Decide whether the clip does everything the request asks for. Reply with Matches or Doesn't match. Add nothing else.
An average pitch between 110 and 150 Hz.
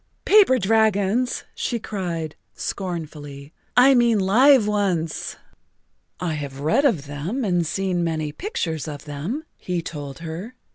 Doesn't match